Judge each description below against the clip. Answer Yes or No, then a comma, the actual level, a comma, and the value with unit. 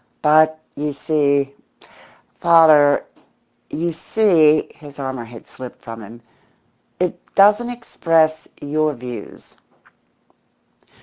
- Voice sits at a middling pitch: Yes, medium, 150 Hz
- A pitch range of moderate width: Yes, average, 3.1 semitones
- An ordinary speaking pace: No, slow, 95 wpm